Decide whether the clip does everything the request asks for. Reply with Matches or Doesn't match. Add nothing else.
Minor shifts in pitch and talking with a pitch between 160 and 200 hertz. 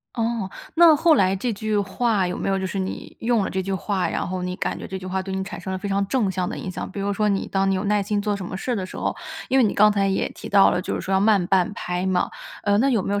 Matches